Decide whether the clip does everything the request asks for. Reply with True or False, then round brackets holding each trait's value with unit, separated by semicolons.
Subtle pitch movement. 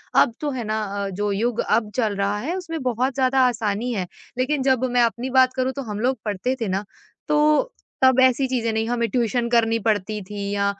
False (3.8 semitones)